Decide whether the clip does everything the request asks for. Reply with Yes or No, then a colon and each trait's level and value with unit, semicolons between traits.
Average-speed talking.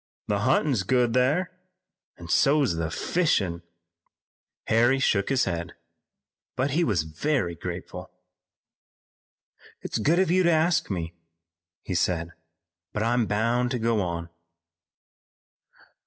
No: slow, 120 wpm